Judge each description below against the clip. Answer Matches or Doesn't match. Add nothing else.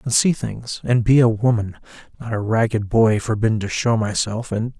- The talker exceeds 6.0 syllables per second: Doesn't match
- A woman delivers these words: Doesn't match